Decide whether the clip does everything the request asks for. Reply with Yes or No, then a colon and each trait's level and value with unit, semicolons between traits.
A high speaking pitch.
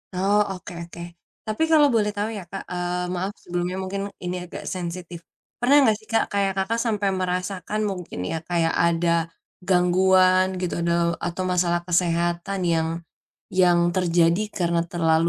No: medium, 180 Hz